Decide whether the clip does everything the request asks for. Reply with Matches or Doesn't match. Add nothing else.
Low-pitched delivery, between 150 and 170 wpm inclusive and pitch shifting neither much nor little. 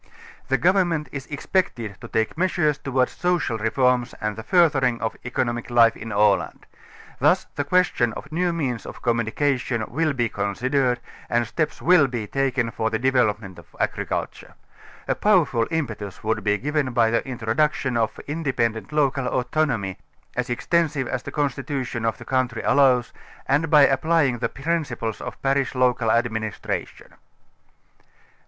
Matches